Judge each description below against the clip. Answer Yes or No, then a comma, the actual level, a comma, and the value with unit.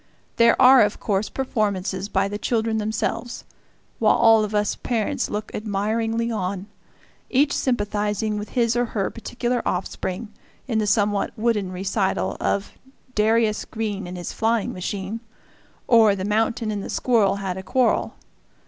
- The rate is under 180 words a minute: Yes, average, 150 wpm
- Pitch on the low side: No, high, 215 Hz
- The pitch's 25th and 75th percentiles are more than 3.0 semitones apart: No, narrow, 2.5 semitones